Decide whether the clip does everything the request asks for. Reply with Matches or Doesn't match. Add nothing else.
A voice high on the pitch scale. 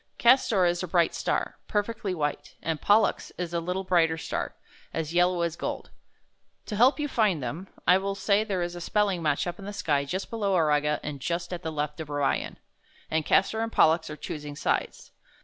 Doesn't match